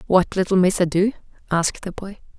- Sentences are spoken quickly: No, average, 175 wpm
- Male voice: No, female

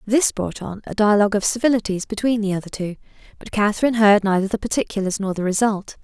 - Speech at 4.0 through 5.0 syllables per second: No, 6.5 syllables/s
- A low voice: No, high, 210 Hz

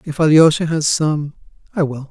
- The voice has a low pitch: No, medium, 155 Hz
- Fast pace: No, average, 170 wpm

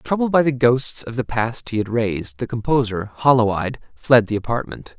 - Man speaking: Yes, male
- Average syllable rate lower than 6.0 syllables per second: Yes, 5.0 syllables/s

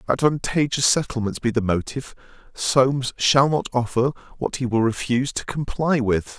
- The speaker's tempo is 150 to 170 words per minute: Yes, average, 160 wpm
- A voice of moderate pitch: No, low, 125 Hz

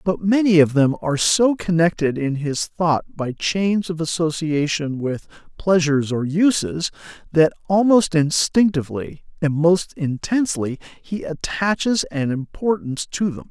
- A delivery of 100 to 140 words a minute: Yes, slow, 135 wpm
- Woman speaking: No, male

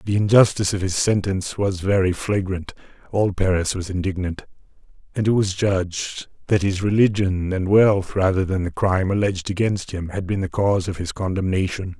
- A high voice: No, very low, 95 Hz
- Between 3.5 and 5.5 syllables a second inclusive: Yes, 5.4 syllables/s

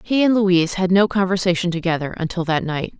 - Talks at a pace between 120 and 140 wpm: No, average, 200 wpm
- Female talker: Yes, female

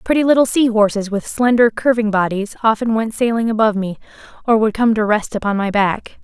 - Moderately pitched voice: No, high, 220 Hz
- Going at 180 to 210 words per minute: Yes, average, 200 wpm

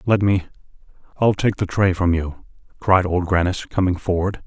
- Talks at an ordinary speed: Yes, average, 160 wpm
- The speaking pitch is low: Yes, very low, 90 Hz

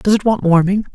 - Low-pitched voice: No, high, 195 Hz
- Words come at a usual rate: No, fast, 255 wpm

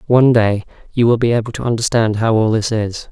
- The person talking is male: Yes, male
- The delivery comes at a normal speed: No, fast, 230 wpm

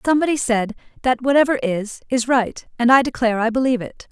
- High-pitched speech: Yes, high, 245 Hz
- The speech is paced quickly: No, average, 190 wpm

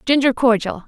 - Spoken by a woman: Yes, female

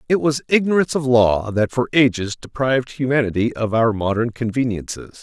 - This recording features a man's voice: Yes, male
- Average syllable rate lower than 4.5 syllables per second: No, 5.5 syllables/s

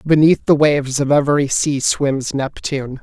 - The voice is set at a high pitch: No, medium, 140 Hz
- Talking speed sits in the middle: Yes, average, 160 wpm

